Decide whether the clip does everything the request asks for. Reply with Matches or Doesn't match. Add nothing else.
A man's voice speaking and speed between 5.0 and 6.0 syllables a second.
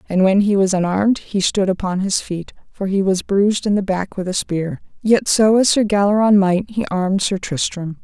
Doesn't match